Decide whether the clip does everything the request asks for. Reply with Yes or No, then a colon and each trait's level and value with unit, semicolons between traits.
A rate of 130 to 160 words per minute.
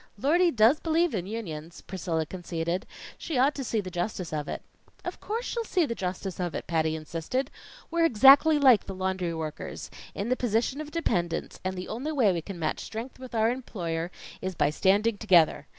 No: average, 195 wpm